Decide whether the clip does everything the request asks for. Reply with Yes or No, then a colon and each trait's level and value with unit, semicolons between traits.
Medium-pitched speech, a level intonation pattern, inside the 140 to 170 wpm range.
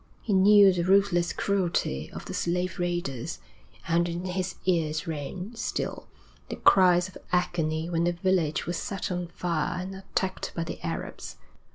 Yes: medium, 175 Hz; narrow, 1.9 semitones; average, 160 wpm